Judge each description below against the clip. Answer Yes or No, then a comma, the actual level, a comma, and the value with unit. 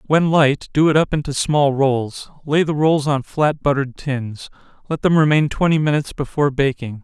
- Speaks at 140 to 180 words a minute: Yes, average, 170 wpm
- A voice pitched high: No, medium, 145 Hz